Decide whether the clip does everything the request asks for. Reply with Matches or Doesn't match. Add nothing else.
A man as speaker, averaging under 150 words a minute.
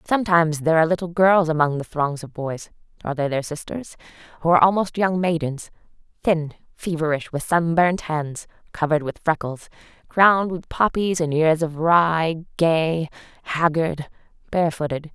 Doesn't match